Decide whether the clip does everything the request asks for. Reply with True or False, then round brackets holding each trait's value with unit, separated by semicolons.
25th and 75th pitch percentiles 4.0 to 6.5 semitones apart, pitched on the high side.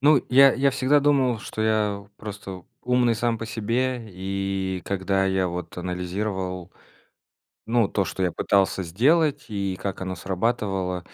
False (4.5 semitones; 100 Hz)